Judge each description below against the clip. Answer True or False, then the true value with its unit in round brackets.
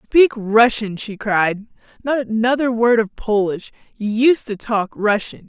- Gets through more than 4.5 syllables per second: False (4.0 syllables/s)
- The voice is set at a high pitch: True (225 Hz)